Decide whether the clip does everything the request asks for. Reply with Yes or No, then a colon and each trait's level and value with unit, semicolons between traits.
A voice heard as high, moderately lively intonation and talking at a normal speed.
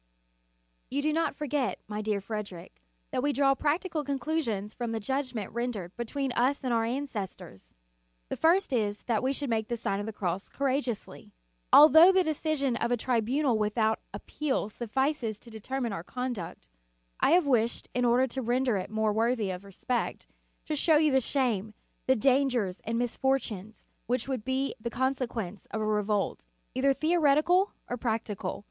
Yes: high, 245 Hz; average, 4.3 semitones; average, 170 wpm